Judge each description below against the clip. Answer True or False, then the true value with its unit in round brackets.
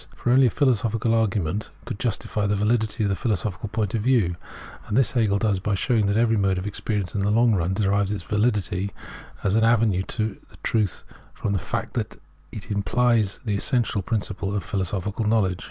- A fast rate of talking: False (190 wpm)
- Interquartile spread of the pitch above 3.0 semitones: False (2.4 semitones)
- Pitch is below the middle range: True (105 Hz)